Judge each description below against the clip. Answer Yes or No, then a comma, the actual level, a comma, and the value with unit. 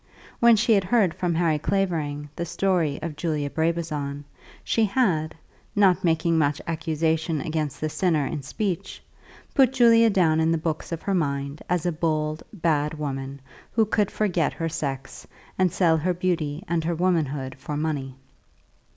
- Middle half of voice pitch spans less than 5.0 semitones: Yes, average, 3.3 semitones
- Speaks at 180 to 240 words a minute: No, average, 160 wpm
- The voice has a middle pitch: Yes, medium, 160 Hz